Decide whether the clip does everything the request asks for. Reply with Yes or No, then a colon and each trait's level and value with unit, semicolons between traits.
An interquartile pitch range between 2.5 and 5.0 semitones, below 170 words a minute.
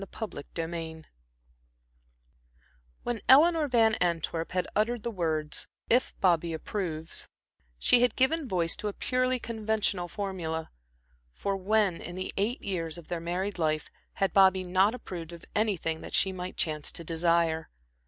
Yes: average, 4.7 semitones; average, 145 wpm